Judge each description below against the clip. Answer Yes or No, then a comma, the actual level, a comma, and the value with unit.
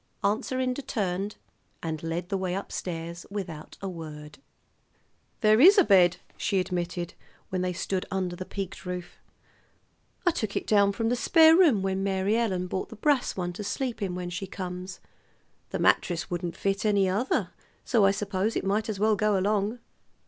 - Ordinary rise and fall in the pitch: Yes, average, 3.0 semitones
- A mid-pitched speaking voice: No, high, 195 Hz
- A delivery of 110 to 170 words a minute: No, average, 180 wpm